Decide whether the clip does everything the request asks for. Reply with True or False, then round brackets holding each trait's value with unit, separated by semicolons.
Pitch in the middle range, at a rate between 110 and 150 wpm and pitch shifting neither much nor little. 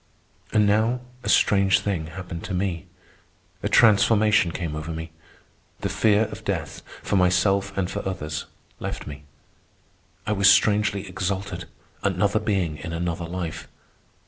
False (95 Hz; 140 wpm; 3.2 semitones)